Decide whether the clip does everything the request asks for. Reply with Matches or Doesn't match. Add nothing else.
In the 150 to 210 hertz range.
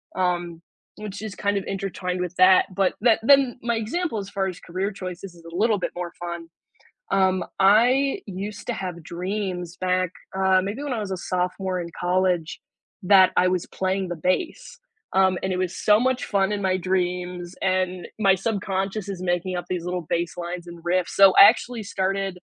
Matches